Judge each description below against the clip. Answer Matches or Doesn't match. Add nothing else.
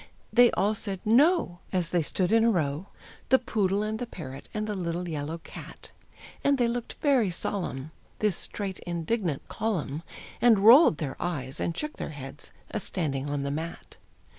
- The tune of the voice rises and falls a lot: Matches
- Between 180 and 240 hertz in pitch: Matches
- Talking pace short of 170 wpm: Doesn't match